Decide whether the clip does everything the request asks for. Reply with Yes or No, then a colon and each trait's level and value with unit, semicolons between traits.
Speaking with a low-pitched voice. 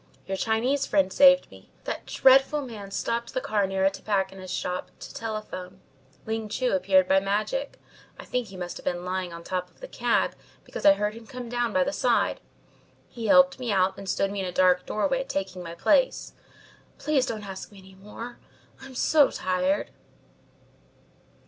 No: high, 210 Hz